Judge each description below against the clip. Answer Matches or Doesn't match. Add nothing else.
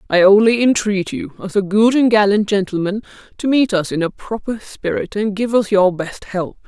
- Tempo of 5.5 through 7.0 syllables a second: Doesn't match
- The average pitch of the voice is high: Matches